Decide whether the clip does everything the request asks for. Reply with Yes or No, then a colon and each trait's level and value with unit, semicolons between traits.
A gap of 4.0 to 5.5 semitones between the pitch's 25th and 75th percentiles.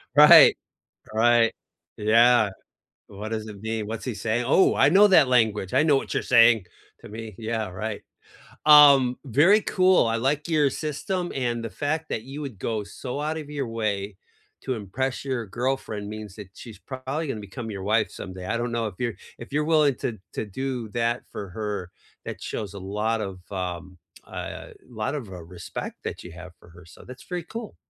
Yes: average, 4.5 semitones